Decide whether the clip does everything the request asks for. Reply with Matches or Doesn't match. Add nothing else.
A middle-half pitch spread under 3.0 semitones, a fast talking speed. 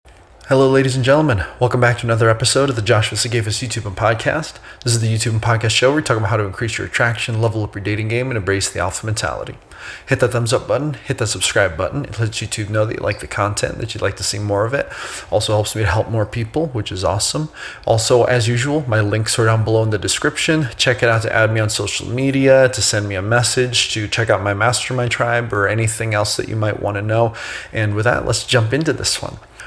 Matches